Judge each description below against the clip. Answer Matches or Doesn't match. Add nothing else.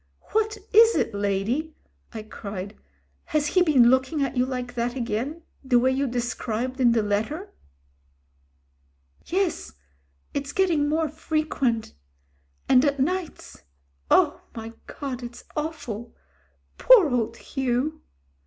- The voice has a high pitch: Matches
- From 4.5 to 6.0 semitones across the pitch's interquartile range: Matches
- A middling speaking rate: Doesn't match